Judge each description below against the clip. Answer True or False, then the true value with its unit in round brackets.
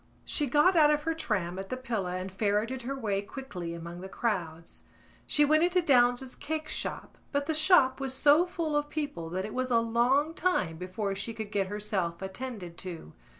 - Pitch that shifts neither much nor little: False (7.5 semitones)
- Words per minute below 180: False (195 wpm)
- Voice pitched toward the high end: True (235 Hz)